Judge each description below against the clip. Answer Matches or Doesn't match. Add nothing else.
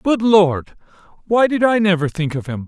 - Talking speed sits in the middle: Matches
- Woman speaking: Doesn't match